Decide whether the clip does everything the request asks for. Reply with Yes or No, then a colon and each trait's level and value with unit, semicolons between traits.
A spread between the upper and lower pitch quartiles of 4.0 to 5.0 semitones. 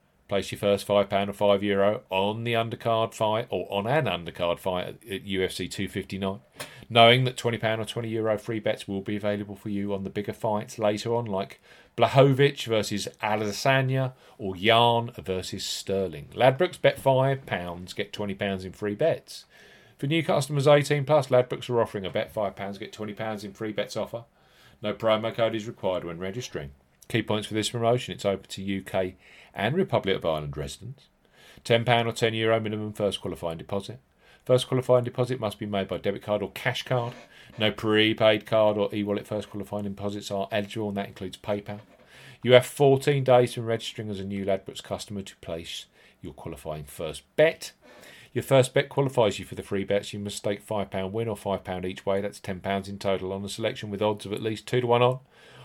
No: average, 3.3 semitones